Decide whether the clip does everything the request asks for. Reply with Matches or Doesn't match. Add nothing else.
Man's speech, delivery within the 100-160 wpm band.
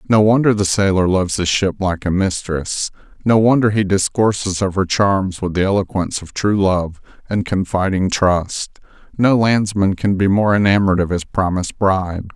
Doesn't match